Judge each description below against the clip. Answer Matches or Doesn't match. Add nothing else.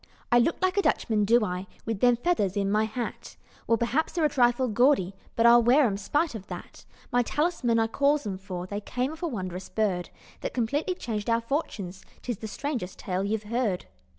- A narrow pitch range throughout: Doesn't match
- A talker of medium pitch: Doesn't match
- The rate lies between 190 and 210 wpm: Matches